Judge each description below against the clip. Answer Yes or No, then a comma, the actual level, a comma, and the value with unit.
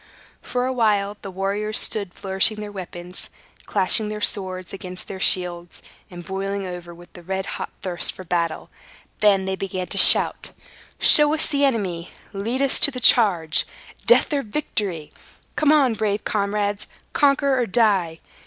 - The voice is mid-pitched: No, high, 200 Hz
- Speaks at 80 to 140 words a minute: No, average, 160 wpm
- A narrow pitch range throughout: No, average, 3.3 semitones